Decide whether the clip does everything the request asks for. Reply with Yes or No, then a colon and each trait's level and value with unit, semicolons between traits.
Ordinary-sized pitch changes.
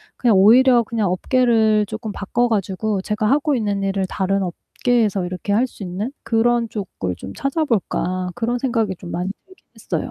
Yes: average, 3.9 semitones